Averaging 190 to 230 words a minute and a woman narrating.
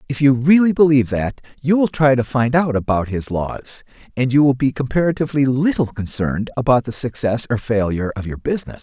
No: average, 195 wpm; male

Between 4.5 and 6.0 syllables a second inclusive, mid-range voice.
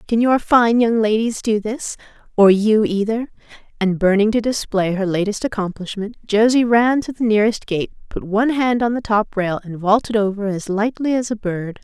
No: 5.0 syllables/s; high, 215 Hz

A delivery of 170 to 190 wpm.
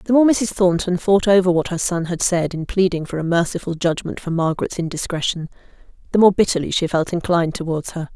No: fast, 205 wpm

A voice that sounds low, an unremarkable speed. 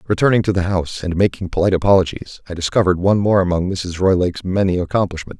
Yes: very low, 95 Hz; average, 190 wpm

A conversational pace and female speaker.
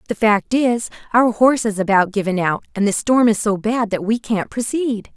No: fast, 220 wpm; female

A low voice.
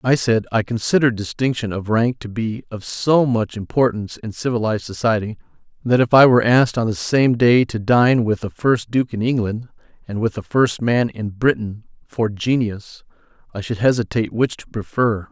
Yes: low, 115 Hz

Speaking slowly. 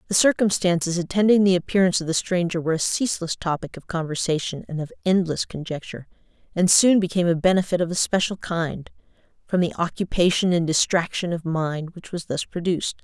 No: average, 175 wpm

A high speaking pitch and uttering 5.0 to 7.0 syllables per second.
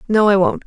Yes: high, 205 Hz; 6.1 syllables/s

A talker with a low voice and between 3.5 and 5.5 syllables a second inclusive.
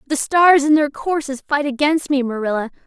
No: very high, 285 Hz; 5.3 syllables/s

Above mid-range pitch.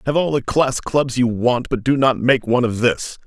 No: low, 125 Hz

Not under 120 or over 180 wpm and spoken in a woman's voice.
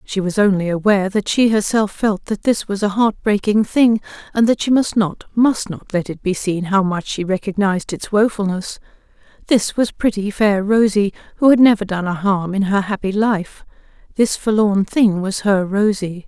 No: average, 190 wpm; female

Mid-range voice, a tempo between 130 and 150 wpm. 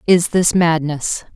Yes: medium, 165 Hz; slow, 135 wpm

